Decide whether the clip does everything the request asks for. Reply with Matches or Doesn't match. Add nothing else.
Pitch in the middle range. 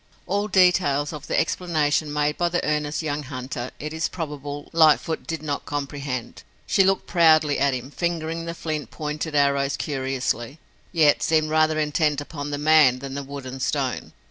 Matches